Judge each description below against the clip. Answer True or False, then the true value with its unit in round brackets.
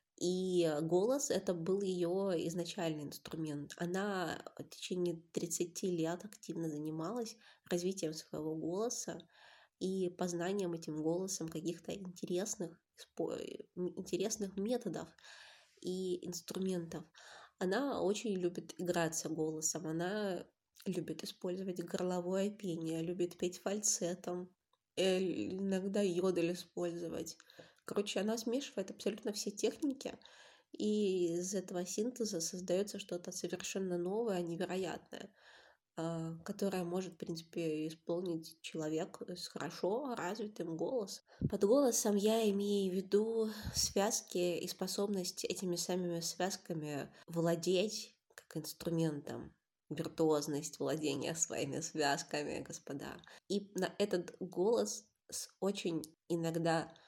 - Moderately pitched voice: True (180 Hz)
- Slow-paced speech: True (100 wpm)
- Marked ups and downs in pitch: False (3.0 semitones)